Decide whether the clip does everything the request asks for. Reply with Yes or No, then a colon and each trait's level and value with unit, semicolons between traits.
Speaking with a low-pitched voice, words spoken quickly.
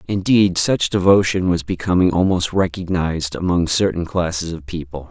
No: very low, 90 Hz; average, 140 wpm